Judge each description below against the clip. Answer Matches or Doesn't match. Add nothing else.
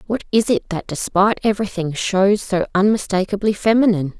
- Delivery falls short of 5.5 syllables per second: Doesn't match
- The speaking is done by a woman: Matches